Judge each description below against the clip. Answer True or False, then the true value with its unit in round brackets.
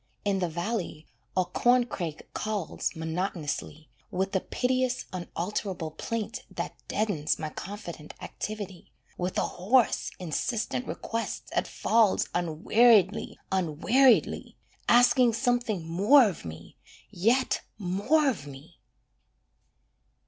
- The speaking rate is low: True (105 wpm)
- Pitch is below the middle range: False (195 Hz)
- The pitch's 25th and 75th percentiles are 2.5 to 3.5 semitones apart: False (5.4 semitones)